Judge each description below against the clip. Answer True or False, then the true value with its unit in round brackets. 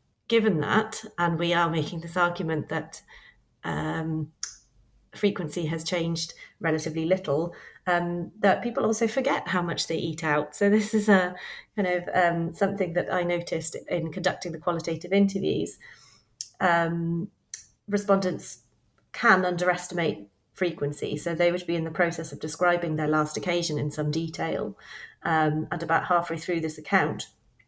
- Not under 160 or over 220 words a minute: False (145 wpm)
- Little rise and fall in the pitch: True (2.3 semitones)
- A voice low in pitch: False (170 Hz)